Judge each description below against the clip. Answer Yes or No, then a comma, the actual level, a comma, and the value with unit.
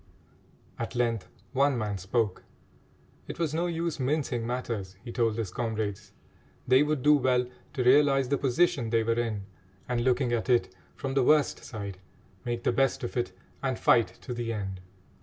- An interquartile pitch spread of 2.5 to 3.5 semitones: Yes, average, 3.1 semitones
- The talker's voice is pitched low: Yes, low, 120 Hz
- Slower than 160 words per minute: No, average, 175 wpm